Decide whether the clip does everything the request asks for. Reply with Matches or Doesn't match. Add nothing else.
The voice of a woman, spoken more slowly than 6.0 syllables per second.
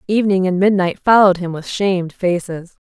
Matches